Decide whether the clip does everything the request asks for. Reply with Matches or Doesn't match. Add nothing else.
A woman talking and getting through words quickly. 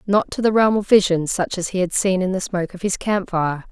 Matches